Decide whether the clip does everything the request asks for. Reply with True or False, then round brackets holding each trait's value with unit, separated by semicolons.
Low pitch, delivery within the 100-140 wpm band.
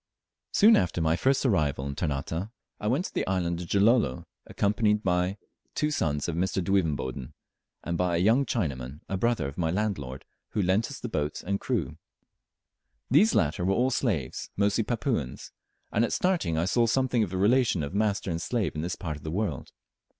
False (95 Hz; 190 wpm)